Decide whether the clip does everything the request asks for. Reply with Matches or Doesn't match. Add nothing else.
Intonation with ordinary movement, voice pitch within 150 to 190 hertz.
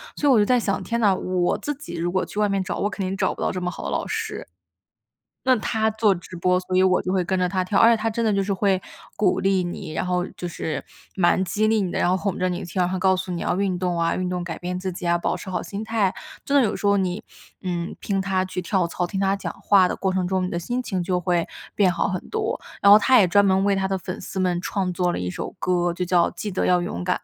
Doesn't match